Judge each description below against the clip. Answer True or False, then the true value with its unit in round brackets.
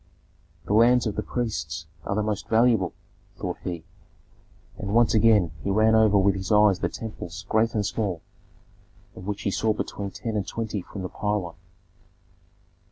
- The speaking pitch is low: True (105 Hz)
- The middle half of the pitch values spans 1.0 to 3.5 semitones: True (2.4 semitones)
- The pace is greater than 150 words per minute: True (165 wpm)